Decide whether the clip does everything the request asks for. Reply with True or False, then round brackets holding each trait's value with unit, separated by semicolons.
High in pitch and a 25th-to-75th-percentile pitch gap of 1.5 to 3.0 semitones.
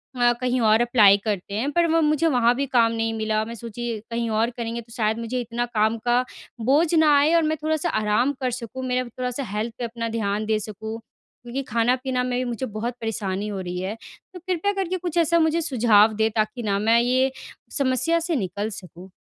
False (235 Hz; 3.4 semitones)